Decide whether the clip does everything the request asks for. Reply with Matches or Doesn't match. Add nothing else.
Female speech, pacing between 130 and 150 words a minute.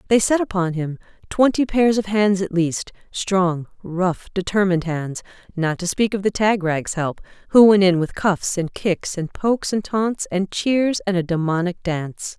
Doesn't match